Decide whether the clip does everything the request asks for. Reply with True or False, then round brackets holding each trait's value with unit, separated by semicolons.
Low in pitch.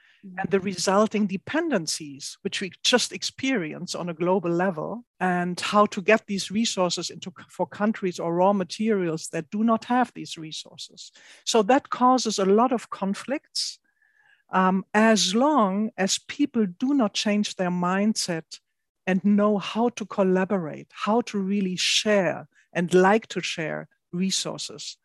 False (200 Hz)